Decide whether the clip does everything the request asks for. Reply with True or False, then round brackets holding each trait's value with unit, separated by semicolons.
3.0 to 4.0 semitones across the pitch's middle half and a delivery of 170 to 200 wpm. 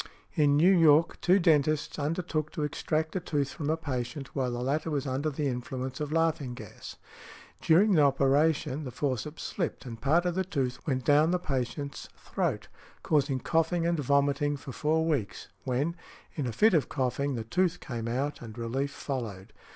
True (3.6 semitones; 175 wpm)